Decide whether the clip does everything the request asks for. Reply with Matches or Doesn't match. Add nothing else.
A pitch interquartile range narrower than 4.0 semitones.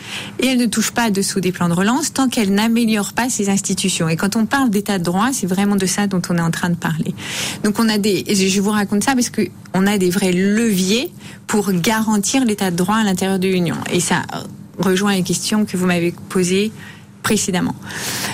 Matches